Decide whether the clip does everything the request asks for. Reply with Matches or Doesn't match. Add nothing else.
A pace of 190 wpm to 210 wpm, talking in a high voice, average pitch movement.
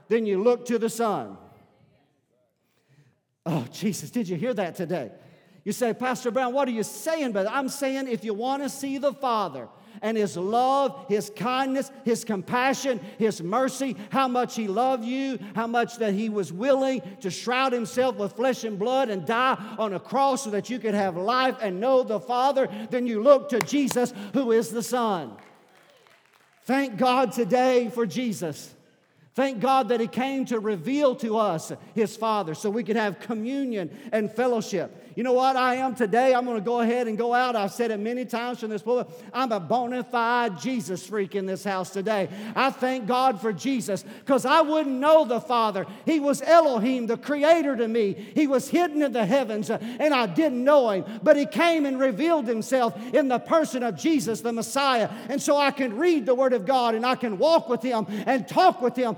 Matches